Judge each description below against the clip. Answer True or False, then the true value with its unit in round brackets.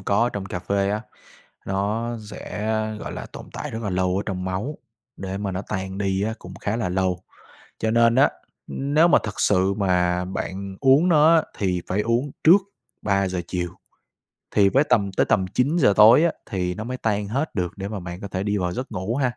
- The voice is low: True (100 Hz)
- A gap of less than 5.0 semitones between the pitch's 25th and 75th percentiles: True (3.8 semitones)